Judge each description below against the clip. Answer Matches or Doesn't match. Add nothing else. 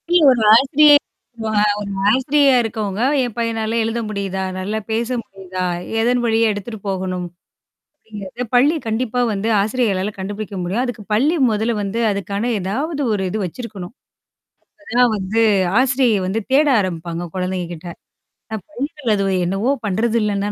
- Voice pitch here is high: Matches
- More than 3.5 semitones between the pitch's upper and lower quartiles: Matches